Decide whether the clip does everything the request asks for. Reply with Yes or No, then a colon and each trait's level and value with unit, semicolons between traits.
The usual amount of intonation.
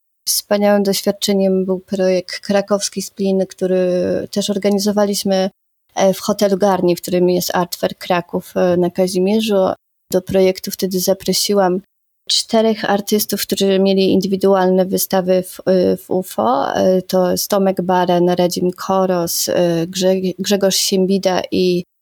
No: narrow, 1.5 semitones